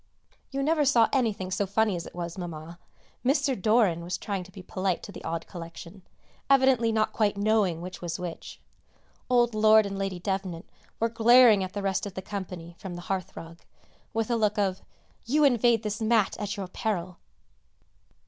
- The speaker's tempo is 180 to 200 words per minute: Yes, average, 185 wpm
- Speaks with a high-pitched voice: Yes, high, 200 Hz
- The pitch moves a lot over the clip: No, average, 3.8 semitones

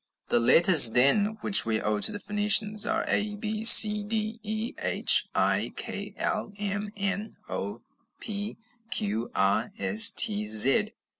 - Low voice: No, high, 205 Hz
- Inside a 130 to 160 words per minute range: Yes, average, 150 wpm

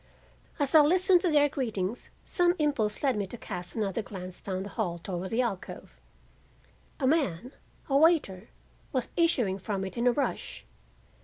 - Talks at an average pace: Yes, average, 155 wpm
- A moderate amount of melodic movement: No, wide, 7.3 semitones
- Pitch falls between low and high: No, high, 235 Hz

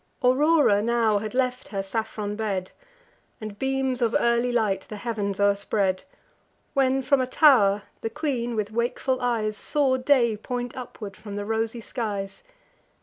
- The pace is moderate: Yes, average, 145 wpm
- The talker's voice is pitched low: No, high, 230 Hz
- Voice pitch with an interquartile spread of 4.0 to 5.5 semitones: No, average, 3.5 semitones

